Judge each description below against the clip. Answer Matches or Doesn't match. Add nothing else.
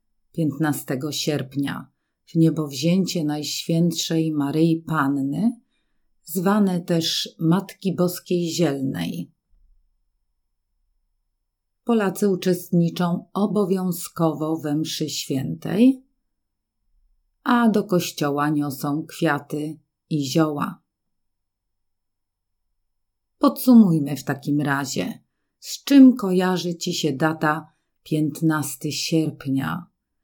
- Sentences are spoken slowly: Matches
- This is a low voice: Doesn't match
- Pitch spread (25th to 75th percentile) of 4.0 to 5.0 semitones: Matches